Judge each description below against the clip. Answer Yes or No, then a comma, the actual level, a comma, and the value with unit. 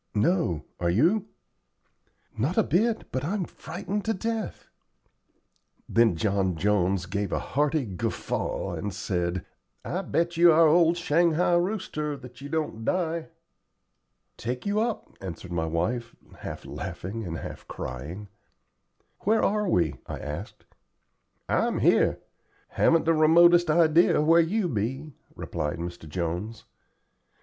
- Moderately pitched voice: Yes, medium, 145 Hz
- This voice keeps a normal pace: No, slow, 130 wpm